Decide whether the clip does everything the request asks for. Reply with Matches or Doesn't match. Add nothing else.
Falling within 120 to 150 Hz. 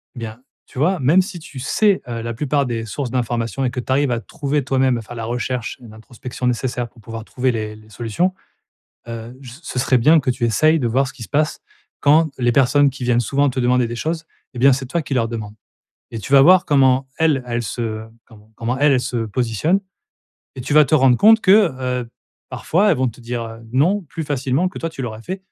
Matches